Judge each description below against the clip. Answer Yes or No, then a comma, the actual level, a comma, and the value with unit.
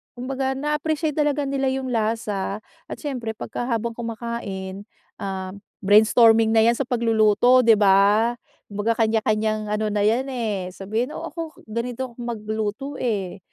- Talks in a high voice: Yes, high, 225 Hz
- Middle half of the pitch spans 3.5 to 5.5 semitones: No, average, 3.1 semitones